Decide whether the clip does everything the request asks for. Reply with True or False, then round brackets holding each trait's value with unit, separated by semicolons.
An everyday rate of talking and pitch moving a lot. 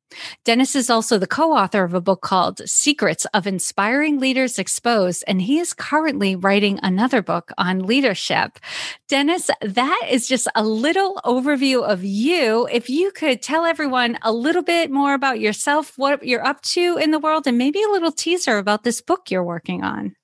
True (185 wpm; 6.3 semitones)